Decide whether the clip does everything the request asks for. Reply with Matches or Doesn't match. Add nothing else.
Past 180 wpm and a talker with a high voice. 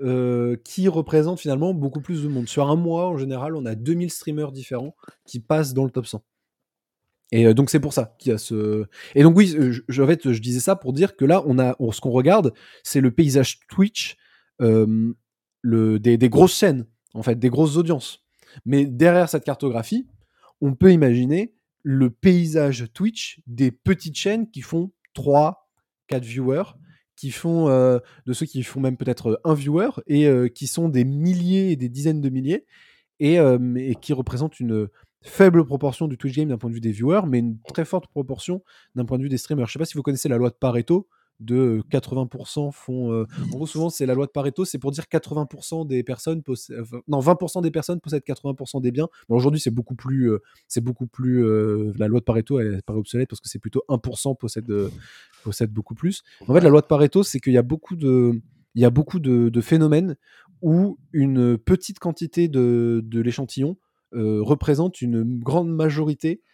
Doesn't match